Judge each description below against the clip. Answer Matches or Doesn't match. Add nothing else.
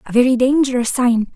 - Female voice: Matches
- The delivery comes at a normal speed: Matches